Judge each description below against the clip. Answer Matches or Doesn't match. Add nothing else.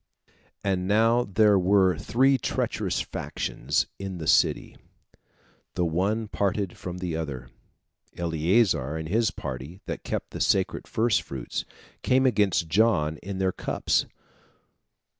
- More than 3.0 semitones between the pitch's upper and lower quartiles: Matches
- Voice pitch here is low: Matches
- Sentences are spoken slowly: Matches